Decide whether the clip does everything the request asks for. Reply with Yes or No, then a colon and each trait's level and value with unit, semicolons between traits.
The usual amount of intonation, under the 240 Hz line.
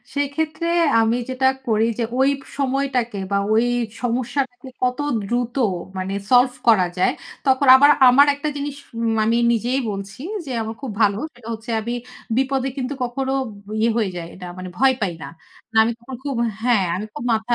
No: average, 3.3 semitones; high, 245 Hz